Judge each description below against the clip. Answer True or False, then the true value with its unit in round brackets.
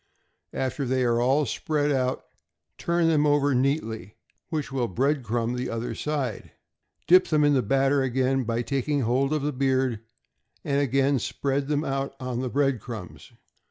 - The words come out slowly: False (165 wpm)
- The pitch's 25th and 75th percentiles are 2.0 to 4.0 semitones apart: True (2.5 semitones)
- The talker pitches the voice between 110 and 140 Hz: True (135 Hz)